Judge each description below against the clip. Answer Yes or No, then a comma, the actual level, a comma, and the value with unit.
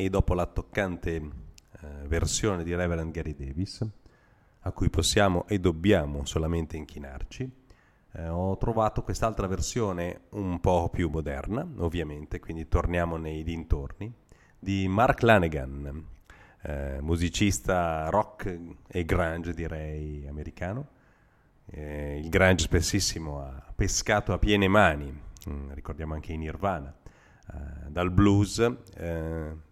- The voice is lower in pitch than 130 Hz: Yes, very low, 85 Hz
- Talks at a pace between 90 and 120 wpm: Yes, slow, 115 wpm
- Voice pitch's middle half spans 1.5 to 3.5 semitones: No, average, 4.1 semitones